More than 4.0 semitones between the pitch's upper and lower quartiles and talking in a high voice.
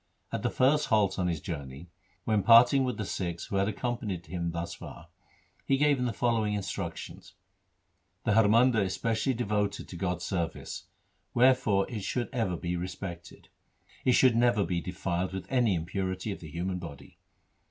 No: average, 4.8 semitones; low, 100 Hz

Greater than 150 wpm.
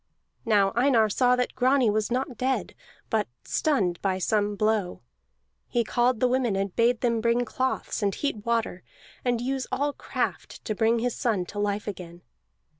Yes: average, 170 wpm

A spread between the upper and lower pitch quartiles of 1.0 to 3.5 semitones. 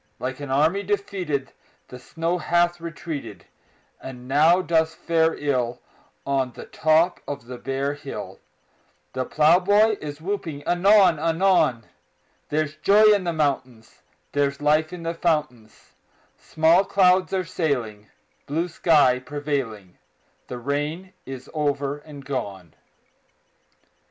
No: average, 4.4 semitones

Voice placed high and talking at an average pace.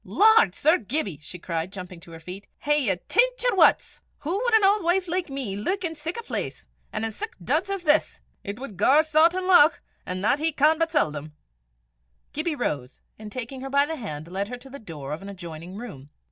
No: very high, 270 Hz; fast, 220 wpm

